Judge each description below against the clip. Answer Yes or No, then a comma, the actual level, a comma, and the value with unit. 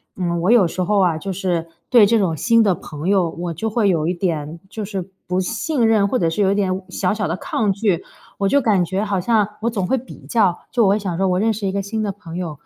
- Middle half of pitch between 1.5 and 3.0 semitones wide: No, average, 3.5 semitones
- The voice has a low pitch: No, high, 195 Hz